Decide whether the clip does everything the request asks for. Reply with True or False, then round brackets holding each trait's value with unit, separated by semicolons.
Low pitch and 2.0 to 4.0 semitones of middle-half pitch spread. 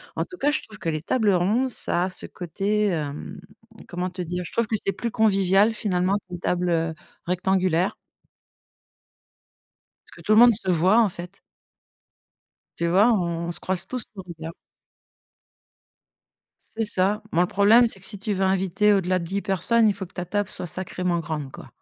False (190 Hz; 3.0 semitones)